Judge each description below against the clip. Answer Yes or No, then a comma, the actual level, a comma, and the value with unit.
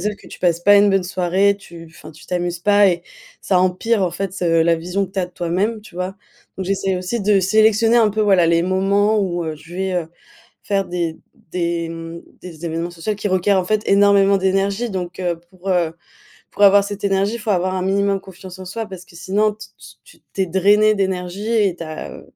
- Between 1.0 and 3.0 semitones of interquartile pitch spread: Yes, narrow, 2.5 semitones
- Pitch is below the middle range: No, high, 190 Hz